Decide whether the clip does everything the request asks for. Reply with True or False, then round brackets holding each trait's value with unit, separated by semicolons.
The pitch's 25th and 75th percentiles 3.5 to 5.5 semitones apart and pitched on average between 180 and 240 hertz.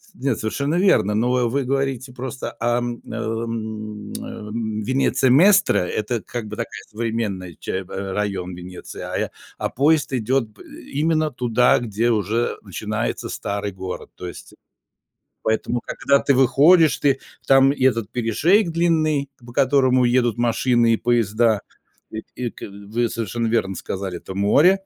False (4.0 semitones; 120 Hz)